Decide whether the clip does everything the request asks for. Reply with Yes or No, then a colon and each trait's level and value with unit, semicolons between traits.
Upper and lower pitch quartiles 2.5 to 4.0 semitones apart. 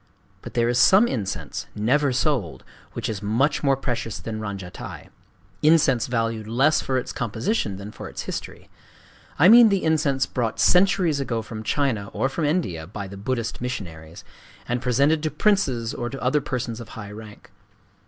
No: average, 5.2 semitones